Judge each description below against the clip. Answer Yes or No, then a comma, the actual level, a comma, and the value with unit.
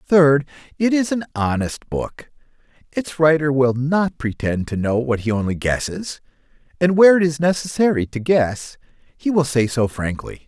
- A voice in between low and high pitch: Yes, medium, 145 Hz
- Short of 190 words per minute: Yes, average, 165 wpm